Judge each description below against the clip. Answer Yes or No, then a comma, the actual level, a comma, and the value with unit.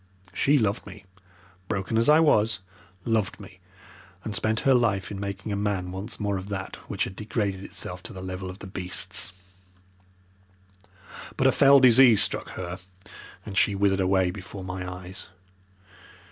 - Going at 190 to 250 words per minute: No, average, 160 wpm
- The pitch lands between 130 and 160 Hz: No, low, 100 Hz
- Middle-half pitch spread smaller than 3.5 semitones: Yes, average, 2.9 semitones